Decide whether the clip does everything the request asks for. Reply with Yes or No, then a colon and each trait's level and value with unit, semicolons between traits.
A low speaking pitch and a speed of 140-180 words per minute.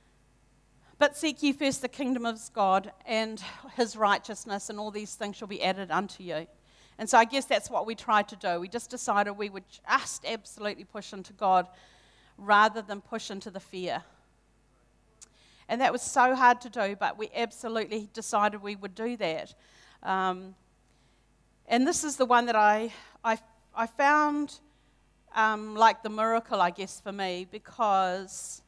No: high, 210 Hz; average, 170 wpm